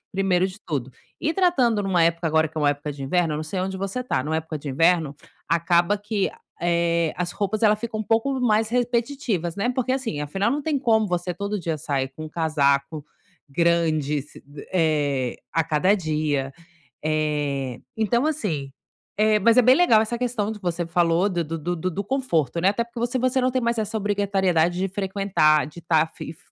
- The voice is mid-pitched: Yes, medium, 180 Hz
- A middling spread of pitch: No, wide, 5.7 semitones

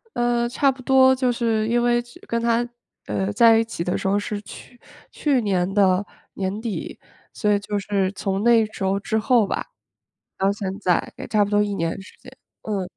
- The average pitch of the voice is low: No, high, 210 Hz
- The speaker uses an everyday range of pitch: Yes, average, 3.4 semitones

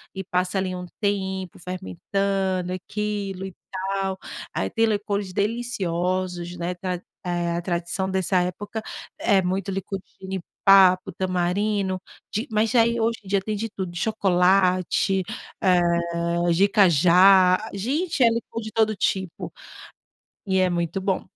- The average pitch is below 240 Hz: Yes, high, 190 Hz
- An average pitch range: No, narrow, 2.1 semitones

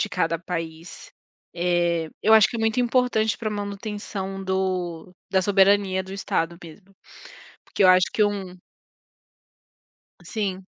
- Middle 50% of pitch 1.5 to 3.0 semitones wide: Yes, narrow, 2.6 semitones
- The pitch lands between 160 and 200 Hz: Yes, high, 190 Hz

